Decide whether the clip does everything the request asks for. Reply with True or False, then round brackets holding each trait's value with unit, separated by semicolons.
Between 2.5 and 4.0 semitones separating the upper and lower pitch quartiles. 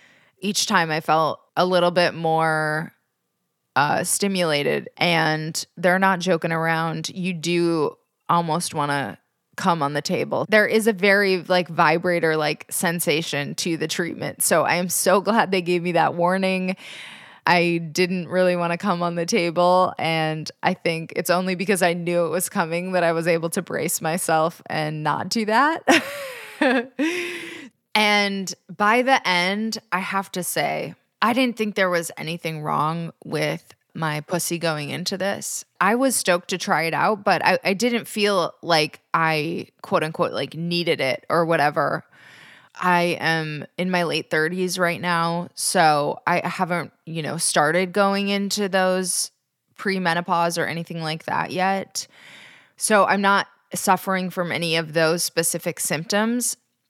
True (2.8 semitones)